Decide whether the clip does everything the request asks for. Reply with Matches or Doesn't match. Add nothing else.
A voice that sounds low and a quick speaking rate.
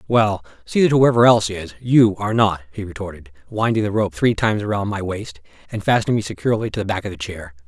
Matches